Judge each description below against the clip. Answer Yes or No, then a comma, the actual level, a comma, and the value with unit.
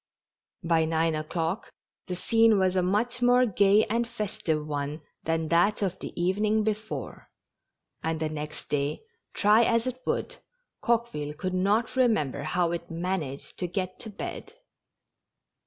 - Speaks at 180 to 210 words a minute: No, average, 155 wpm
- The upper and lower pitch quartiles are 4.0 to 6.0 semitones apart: Yes, average, 5.2 semitones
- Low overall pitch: No, medium, 185 Hz